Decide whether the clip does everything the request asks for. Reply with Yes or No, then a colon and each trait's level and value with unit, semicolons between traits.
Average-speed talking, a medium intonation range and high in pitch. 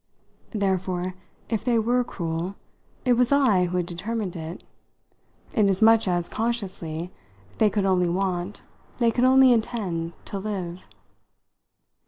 No: slow, 125 wpm; average, 4.4 semitones; high, 195 Hz